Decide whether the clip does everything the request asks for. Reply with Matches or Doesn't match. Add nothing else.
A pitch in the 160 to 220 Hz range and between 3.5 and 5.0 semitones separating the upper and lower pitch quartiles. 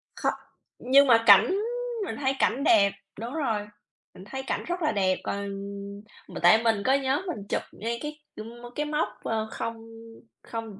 Doesn't match